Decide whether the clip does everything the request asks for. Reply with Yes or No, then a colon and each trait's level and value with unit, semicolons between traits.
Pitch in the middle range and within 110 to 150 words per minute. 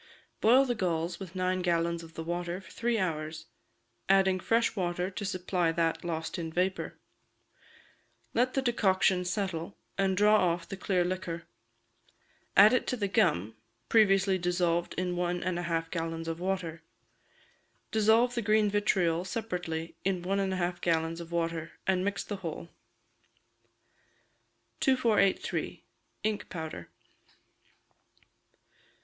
Yes: medium, 180 Hz; slow, 135 wpm